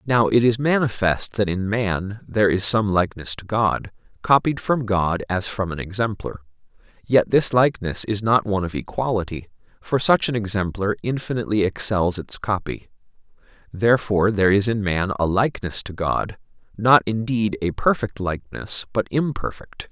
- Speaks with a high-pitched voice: No, low, 105 Hz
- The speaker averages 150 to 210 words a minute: Yes, average, 155 wpm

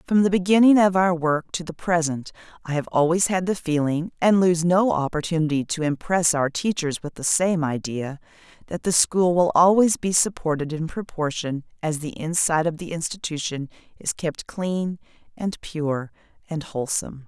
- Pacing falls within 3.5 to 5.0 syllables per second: Yes, 4.9 syllables/s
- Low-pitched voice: No, medium, 165 Hz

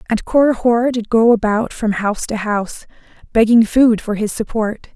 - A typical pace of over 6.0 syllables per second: No, 4.9 syllables/s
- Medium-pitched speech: No, high, 225 Hz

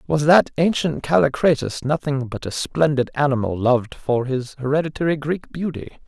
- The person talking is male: Yes, male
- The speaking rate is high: No, average, 150 wpm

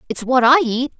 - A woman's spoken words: Yes, female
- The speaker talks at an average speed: No, fast, 240 wpm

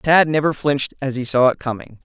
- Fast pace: Yes, fast, 235 wpm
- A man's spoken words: Yes, male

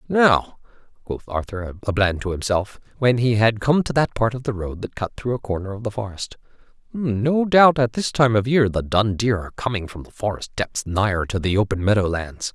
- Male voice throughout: Yes, male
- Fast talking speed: Yes, fast, 225 wpm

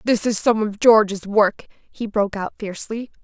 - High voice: Yes, high, 210 Hz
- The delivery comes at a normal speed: Yes, average, 185 wpm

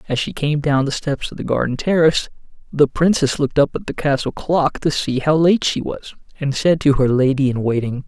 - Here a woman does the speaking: No, male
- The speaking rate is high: Yes, fast, 230 wpm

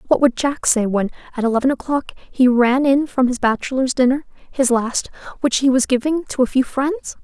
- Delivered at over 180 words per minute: Yes, average, 190 wpm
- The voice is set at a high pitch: Yes, very high, 260 Hz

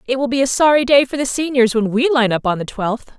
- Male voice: No, female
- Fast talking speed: Yes, fast, 300 wpm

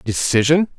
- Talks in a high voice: No, medium, 140 Hz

